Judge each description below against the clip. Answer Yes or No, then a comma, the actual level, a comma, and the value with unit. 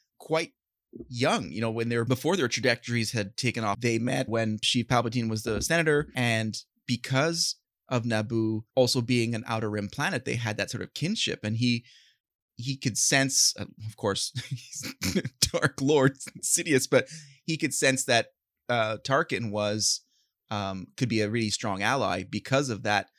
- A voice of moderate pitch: No, low, 120 Hz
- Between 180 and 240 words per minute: No, average, 165 wpm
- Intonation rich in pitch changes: No, average, 3.5 semitones